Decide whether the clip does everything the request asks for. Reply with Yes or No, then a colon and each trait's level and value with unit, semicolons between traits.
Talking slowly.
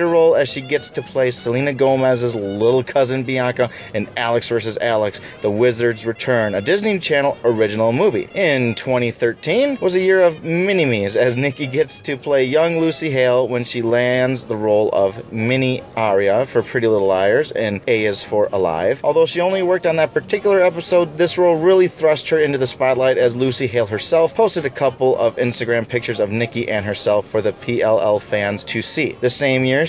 No: average, 190 wpm